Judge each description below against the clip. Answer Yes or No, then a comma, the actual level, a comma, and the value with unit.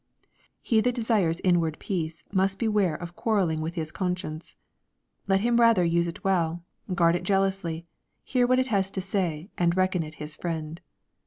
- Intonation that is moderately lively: Yes, average, 3.1 semitones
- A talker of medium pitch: Yes, medium, 180 Hz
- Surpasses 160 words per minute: Yes, average, 175 wpm